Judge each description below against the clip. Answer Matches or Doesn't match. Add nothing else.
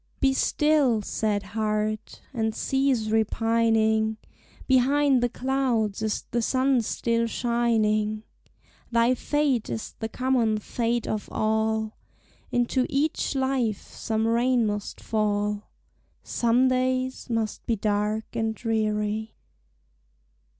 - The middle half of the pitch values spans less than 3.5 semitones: Matches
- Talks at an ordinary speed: Doesn't match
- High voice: Matches